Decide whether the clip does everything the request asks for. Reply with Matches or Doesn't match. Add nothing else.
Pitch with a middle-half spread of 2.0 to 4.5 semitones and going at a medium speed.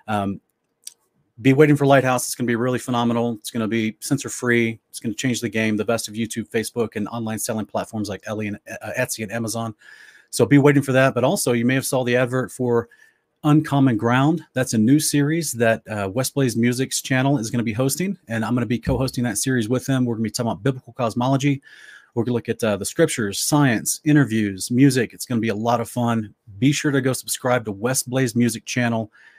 Doesn't match